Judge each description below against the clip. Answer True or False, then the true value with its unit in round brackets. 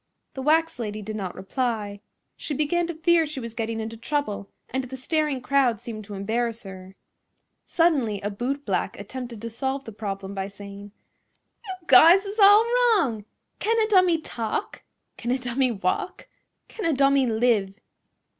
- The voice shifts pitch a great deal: True (6.4 semitones)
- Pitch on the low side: False (245 Hz)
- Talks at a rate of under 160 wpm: False (165 wpm)